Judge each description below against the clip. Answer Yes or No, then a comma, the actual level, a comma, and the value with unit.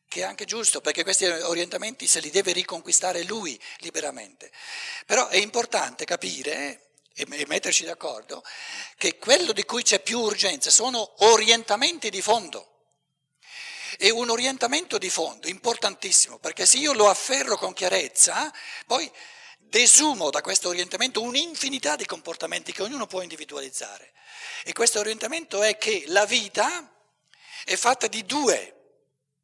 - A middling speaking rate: Yes, average, 135 wpm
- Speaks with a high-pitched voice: Yes, high, 235 Hz